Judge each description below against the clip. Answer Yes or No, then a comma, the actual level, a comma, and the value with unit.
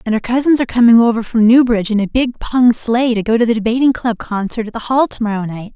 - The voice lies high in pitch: Yes, high, 230 Hz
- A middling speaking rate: No, fast, 260 wpm